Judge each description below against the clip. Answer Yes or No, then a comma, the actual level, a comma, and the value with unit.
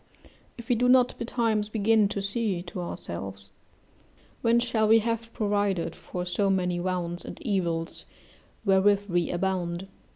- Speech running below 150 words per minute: Yes, average, 140 wpm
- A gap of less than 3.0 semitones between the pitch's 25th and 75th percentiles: No, average, 4.2 semitones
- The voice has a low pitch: No, high, 195 Hz